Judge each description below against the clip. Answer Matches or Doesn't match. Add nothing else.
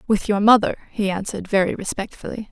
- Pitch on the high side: Matches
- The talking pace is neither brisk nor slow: Matches